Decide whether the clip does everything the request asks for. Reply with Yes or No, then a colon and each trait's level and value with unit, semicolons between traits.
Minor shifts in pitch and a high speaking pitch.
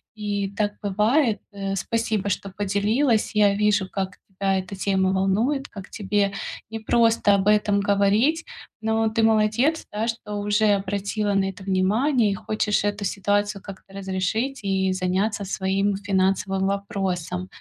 Yes: narrow, 1.9 semitones; high, 205 Hz